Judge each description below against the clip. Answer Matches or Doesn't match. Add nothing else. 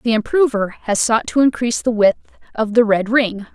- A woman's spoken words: Matches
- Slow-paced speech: Doesn't match